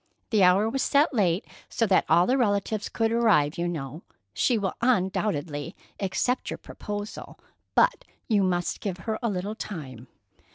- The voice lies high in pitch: Yes, high, 200 Hz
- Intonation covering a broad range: No, average, 4.4 semitones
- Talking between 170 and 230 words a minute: No, average, 160 wpm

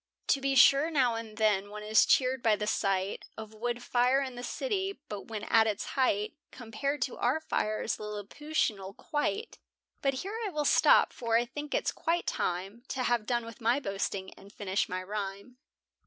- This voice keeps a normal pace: Yes, average, 185 wpm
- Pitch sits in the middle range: No, high, 230 Hz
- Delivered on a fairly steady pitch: No, average, 4.5 semitones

